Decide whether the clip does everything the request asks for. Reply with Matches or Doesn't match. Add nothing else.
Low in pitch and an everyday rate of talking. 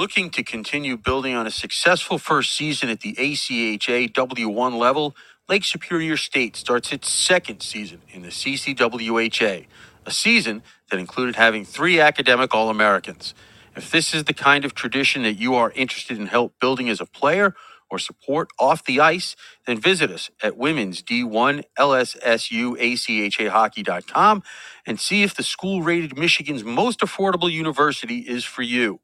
Matches